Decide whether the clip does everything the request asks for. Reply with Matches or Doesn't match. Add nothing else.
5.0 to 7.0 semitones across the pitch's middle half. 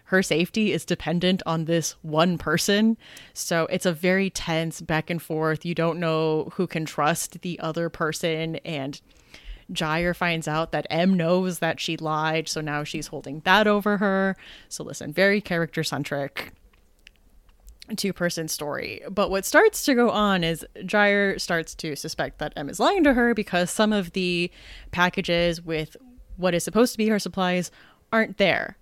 Doesn't match